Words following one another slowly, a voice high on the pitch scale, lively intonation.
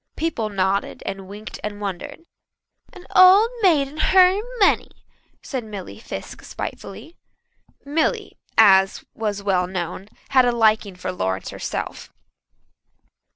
Yes: slow, 120 wpm; high, 215 Hz; wide, 7.8 semitones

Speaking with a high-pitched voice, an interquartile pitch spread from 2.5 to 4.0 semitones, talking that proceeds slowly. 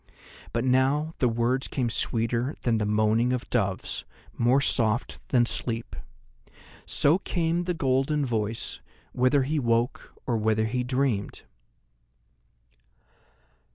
No: low, 125 Hz; average, 2.9 semitones; slow, 120 wpm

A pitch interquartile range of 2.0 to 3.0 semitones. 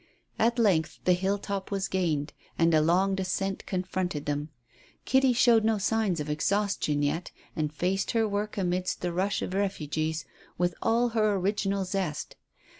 No: average, 3.6 semitones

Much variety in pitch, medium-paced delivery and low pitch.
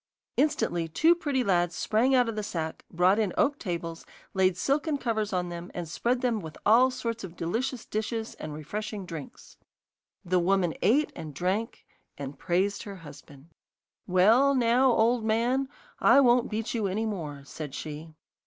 No: wide, 5.9 semitones; average, 165 wpm; high, 210 Hz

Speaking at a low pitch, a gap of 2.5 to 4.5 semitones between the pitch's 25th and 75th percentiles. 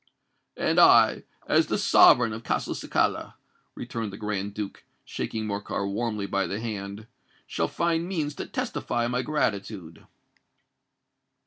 Yes: low, 110 Hz; average, 3.1 semitones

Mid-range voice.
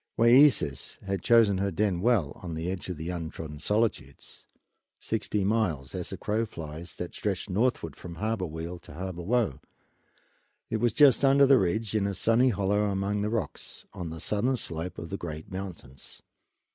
No: very low, 95 Hz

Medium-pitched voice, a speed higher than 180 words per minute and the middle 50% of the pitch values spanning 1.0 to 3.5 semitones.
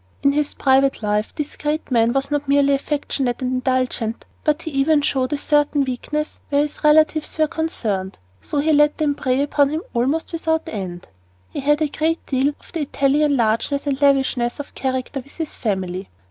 No: very high, 280 Hz; average, 190 wpm; average, 2.7 semitones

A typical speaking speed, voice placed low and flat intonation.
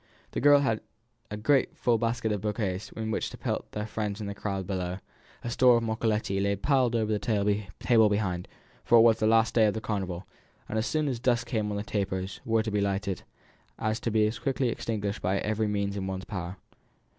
No: fast, 215 wpm; low, 105 Hz; narrow, 2.3 semitones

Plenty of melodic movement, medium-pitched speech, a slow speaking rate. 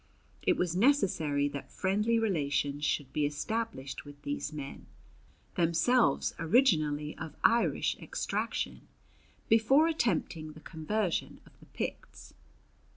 Yes: wide, 7.3 semitones; medium, 160 Hz; slow, 110 wpm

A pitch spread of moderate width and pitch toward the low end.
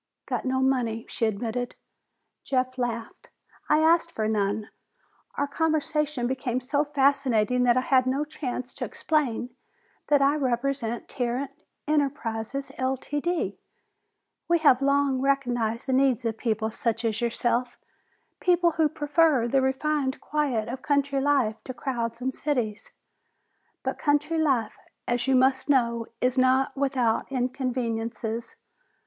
No: average, 3.1 semitones; very high, 260 Hz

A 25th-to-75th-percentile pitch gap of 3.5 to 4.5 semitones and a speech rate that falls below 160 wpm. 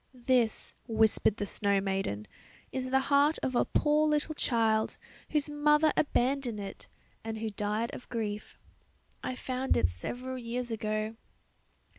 Yes: average, 3.8 semitones; average, 140 wpm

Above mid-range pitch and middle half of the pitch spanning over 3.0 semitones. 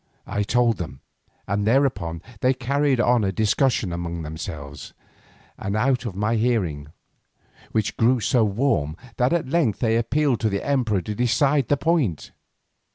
No: low, 115 Hz; average, 5.2 semitones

